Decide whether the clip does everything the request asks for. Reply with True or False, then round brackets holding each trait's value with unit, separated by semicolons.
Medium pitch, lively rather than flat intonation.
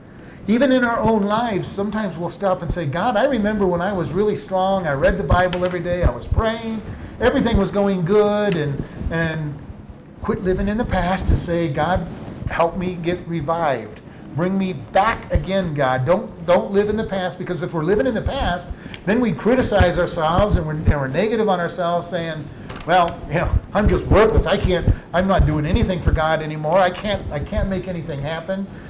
False (180 Hz; 3.6 semitones)